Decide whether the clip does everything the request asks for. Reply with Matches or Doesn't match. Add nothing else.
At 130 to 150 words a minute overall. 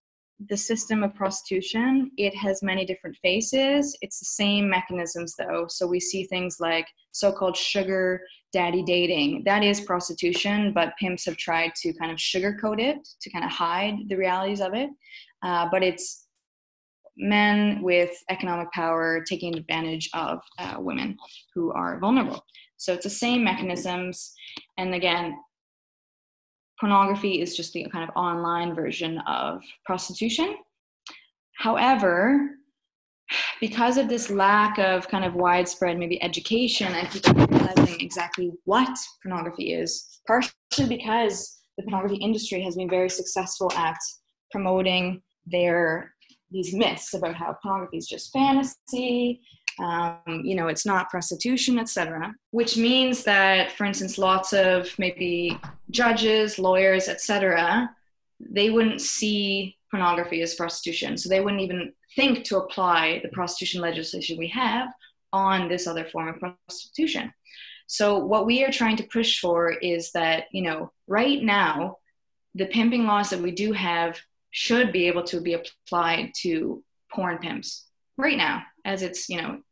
Matches